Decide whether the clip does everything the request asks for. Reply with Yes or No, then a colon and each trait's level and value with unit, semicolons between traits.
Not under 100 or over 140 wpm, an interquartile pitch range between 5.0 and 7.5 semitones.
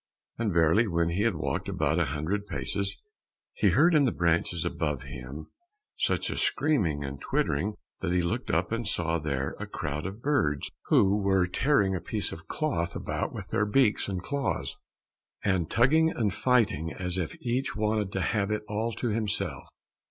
No: average, 180 wpm; wide, 5.4 semitones